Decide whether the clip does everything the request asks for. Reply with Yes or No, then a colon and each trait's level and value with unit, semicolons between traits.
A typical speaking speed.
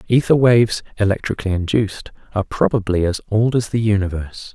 Yes: average, 145 wpm